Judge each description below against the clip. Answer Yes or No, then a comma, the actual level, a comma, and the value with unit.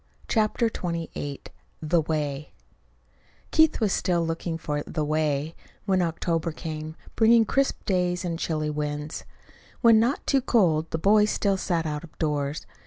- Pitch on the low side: No, medium, 165 Hz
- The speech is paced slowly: No, average, 145 wpm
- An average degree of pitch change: Yes, average, 4.5 semitones